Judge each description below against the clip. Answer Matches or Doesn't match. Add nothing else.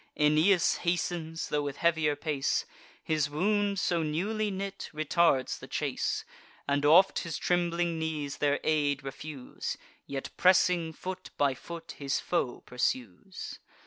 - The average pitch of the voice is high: Doesn't match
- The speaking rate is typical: Doesn't match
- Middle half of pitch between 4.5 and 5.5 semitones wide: Doesn't match